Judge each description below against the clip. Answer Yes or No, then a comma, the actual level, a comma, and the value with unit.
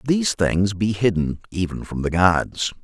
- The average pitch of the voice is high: No, very low, 95 Hz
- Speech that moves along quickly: No, average, 170 wpm